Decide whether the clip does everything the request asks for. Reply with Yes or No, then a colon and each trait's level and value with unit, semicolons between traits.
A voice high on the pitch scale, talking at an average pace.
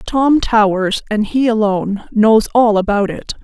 Yes: high, 215 Hz; average, 155 wpm